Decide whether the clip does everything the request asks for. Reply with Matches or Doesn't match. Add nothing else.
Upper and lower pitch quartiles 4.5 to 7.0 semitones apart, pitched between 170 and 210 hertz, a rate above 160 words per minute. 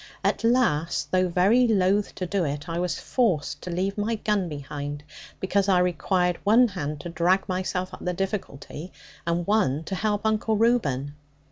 Doesn't match